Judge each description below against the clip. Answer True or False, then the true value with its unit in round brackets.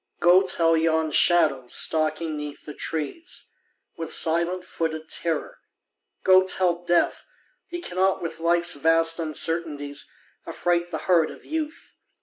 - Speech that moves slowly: True (130 wpm)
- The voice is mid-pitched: True (165 Hz)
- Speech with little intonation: True (1.8 semitones)